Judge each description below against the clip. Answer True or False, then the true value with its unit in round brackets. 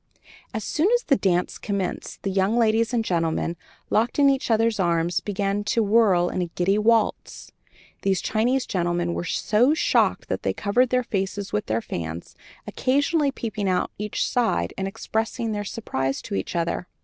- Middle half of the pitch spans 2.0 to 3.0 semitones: False (4.6 semitones)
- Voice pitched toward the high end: True (205 Hz)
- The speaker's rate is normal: True (175 wpm)